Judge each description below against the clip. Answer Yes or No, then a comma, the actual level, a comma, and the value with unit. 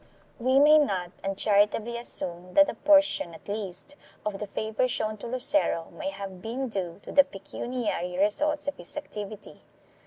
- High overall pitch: Yes, high, 210 Hz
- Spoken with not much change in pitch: No, average, 5.0 semitones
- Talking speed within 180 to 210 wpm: No, average, 165 wpm